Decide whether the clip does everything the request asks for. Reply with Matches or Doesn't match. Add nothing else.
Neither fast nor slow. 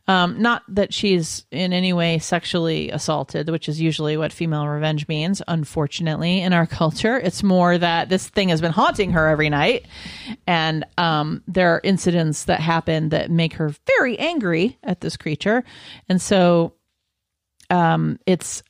Matches